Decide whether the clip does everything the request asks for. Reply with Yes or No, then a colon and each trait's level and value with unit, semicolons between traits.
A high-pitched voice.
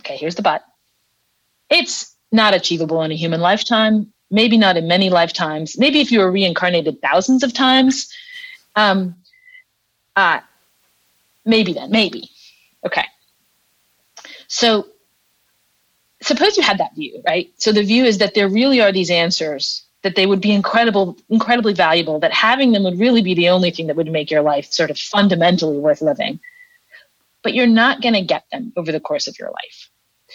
Yes: high, 205 Hz